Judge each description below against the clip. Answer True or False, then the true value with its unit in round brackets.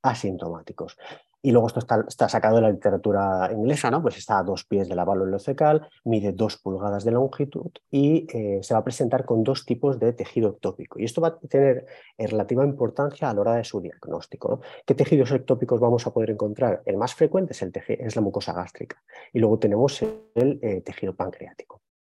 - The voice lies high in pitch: False (120 Hz)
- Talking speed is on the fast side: True (205 wpm)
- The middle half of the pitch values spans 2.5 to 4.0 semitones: False (4.7 semitones)